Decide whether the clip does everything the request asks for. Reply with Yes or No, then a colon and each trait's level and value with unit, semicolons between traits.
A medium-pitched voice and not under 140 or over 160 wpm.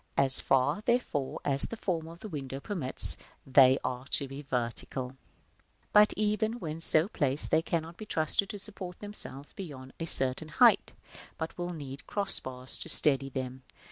No: medium, 150 Hz; average, 175 wpm